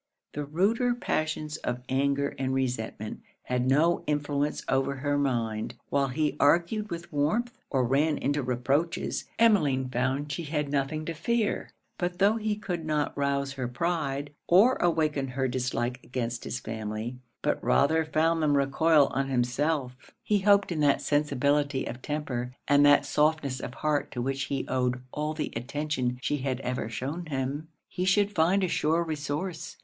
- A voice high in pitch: No, medium, 145 Hz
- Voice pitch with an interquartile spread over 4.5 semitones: No, average, 3.5 semitones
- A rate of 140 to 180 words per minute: Yes, average, 165 wpm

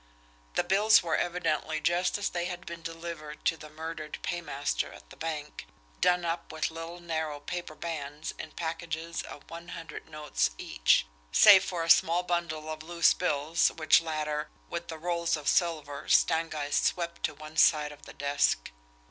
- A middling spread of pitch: No, narrow, 2.0 semitones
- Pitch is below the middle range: No, medium, 165 Hz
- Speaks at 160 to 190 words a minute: Yes, average, 170 wpm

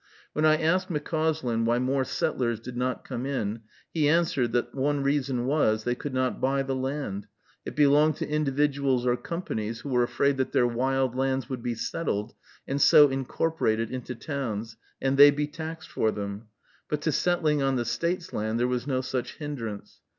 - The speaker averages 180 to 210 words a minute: Yes, average, 185 wpm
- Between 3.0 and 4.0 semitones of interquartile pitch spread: Yes, average, 3.4 semitones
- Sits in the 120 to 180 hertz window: Yes, low, 135 Hz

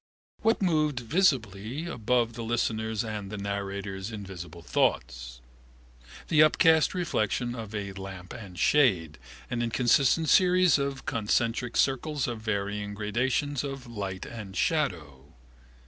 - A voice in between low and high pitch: No, low, 115 Hz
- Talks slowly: Yes, slow, 120 wpm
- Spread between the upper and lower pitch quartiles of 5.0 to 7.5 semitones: Yes, wide, 5.5 semitones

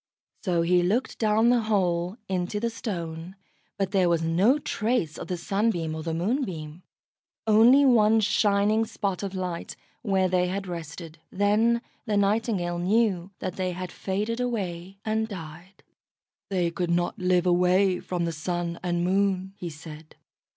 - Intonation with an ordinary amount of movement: Yes, average, 3.5 semitones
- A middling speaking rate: Yes, average, 155 wpm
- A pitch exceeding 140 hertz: Yes, medium, 185 Hz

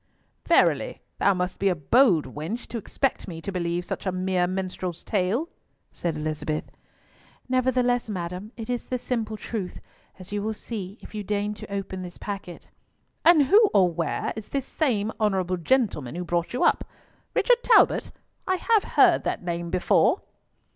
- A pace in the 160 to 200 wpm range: Yes, average, 165 wpm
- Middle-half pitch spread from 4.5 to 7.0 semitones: Yes, average, 5.0 semitones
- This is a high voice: Yes, high, 195 Hz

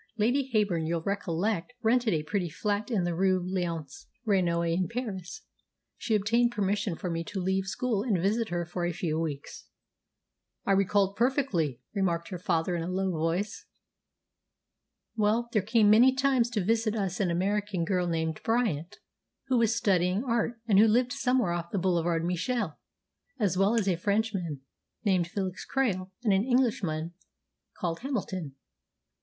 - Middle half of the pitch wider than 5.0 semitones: No, average, 4.4 semitones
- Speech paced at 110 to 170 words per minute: Yes, average, 160 wpm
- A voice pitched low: No, high, 195 Hz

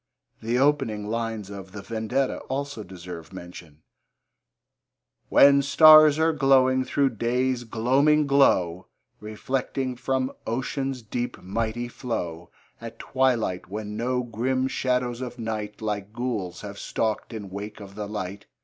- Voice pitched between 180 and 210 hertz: No, low, 115 Hz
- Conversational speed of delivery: No, slow, 130 wpm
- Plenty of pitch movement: No, average, 4.0 semitones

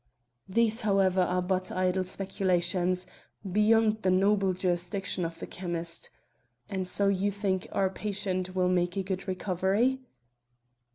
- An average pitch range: No, narrow, 1.6 semitones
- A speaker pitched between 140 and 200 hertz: Yes, high, 190 Hz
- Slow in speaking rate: Yes, slow, 130 wpm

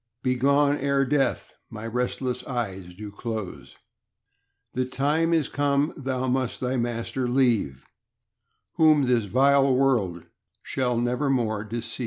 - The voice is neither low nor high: No, low, 125 Hz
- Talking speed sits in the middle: No, slow, 125 wpm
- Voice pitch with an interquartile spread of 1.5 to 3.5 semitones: Yes, average, 3.0 semitones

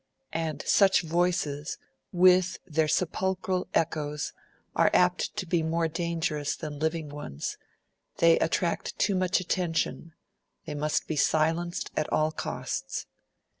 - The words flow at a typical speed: No, slow, 125 wpm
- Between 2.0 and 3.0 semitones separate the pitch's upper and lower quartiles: Yes, narrow, 2.6 semitones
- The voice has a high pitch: No, medium, 165 Hz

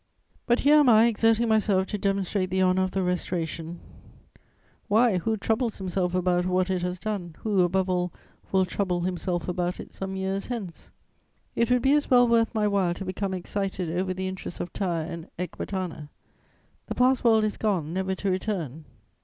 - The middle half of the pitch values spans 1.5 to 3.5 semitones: Yes, average, 3.2 semitones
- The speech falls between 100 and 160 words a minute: No, average, 185 wpm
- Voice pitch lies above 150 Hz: Yes, high, 190 Hz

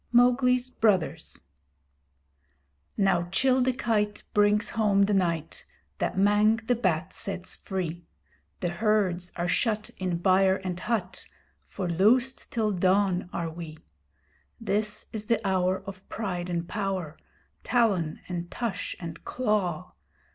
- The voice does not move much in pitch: No, average, 3.4 semitones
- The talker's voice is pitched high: Yes, high, 195 Hz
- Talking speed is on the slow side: Yes, slow, 125 wpm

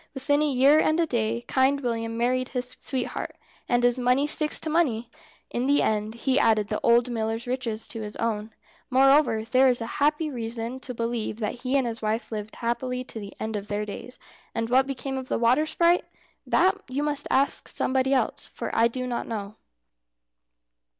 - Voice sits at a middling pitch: No, high, 245 Hz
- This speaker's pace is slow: No, average, 190 wpm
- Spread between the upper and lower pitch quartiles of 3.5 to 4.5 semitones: No, average, 2.9 semitones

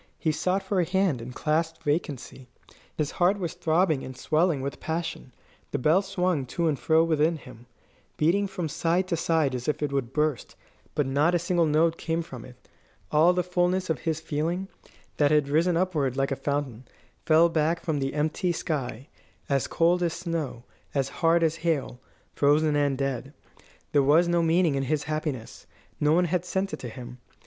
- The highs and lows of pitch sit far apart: No, average, 3.5 semitones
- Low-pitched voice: No, medium, 155 Hz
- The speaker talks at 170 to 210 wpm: Yes, average, 190 wpm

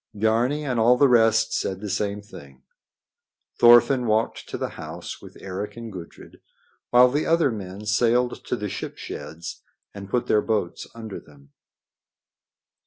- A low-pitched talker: Yes, low, 110 Hz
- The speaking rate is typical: Yes, average, 155 wpm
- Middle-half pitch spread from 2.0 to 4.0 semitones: Yes, average, 3.5 semitones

